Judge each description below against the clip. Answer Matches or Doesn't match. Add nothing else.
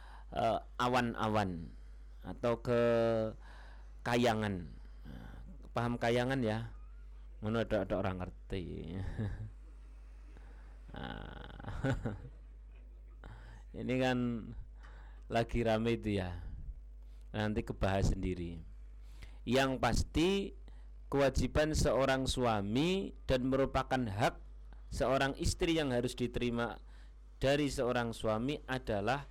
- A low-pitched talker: Matches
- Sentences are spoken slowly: Matches